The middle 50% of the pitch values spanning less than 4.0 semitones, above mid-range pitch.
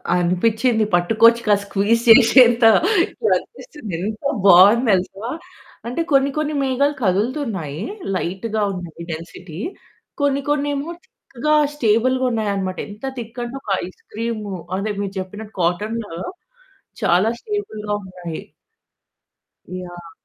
No: average, 5.1 semitones; high, 215 Hz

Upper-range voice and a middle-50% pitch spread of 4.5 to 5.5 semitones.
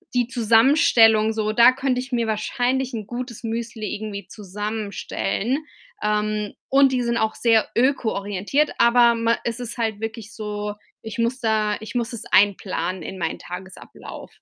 No: high, 225 Hz; narrow, 2.4 semitones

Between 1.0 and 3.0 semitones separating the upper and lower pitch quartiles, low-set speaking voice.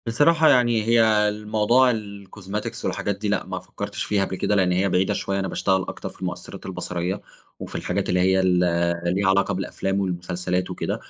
Yes: narrow, 2.4 semitones; low, 100 Hz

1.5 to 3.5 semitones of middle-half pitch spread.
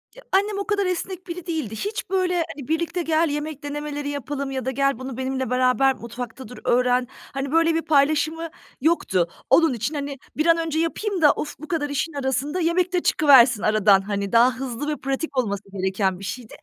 No: average, 4.6 semitones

